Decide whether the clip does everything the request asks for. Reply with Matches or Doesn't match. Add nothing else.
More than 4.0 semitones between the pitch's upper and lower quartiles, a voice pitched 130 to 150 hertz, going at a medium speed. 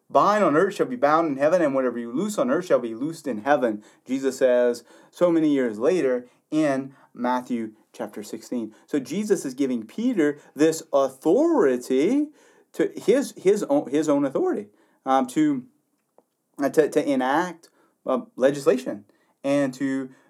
Matches